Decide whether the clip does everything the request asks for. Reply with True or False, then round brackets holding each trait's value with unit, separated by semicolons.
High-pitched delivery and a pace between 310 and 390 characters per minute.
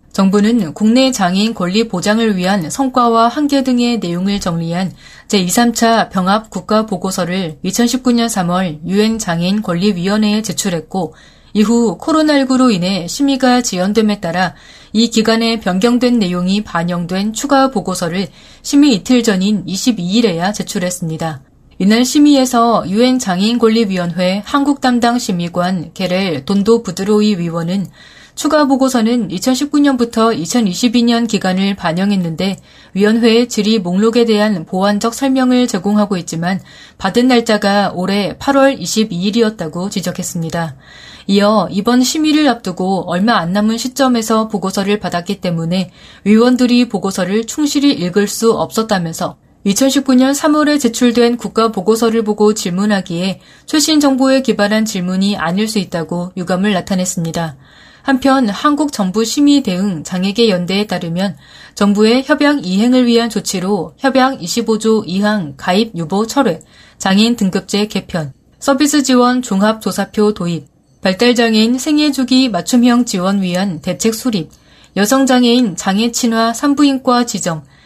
False (210 Hz; 300 characters per minute)